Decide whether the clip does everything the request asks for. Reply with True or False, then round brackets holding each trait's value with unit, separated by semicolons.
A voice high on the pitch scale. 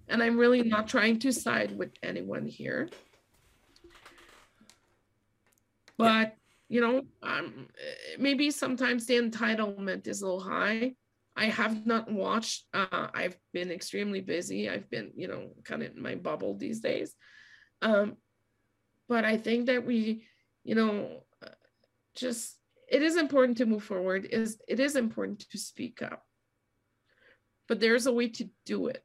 True (225 Hz)